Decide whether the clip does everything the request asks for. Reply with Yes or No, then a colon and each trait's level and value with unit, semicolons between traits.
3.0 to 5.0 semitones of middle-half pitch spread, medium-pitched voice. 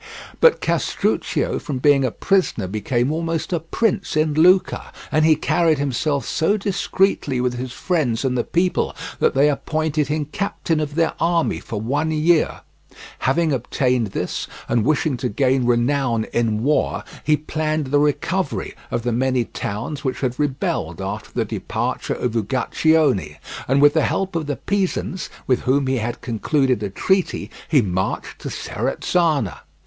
Yes: average, 4.4 semitones; medium, 145 Hz